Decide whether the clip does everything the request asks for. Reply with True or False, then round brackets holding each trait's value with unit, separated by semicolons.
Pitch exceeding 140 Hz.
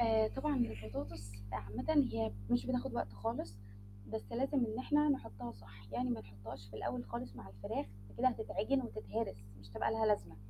False (120 Hz)